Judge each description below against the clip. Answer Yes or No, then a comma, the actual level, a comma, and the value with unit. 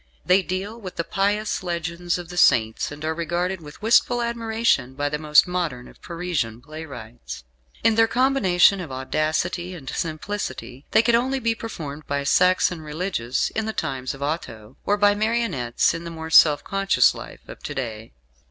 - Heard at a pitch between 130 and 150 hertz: No, medium, 170 Hz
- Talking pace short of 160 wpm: No, average, 175 wpm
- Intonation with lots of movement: Yes, wide, 6.1 semitones